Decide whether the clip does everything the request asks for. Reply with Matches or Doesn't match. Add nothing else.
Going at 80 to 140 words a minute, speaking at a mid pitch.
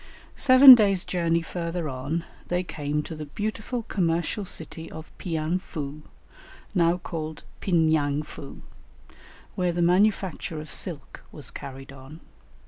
Matches